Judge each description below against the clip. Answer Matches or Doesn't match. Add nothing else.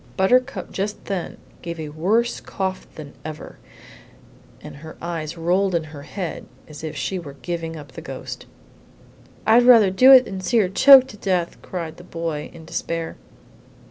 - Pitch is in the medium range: Matches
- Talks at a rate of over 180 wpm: Doesn't match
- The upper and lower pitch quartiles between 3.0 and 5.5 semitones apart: Matches